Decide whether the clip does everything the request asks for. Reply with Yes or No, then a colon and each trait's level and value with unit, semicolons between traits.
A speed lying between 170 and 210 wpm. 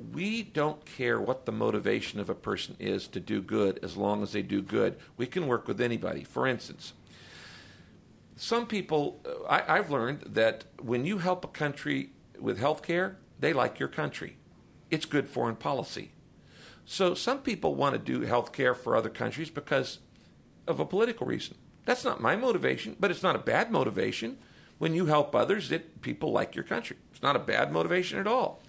Yes: average, 190 wpm